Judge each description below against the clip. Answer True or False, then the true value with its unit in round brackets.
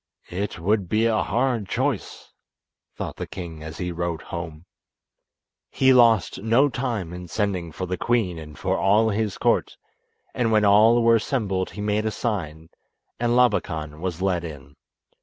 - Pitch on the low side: True (100 Hz)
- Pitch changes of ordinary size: True (4.7 semitones)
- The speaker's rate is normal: True (160 wpm)